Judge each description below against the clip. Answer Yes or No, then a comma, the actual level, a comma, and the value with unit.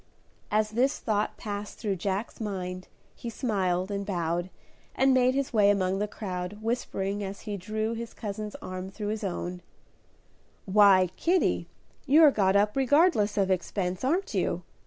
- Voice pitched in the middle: No, high, 205 Hz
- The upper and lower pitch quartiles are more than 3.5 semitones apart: No, average, 3.2 semitones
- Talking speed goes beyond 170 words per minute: No, average, 155 wpm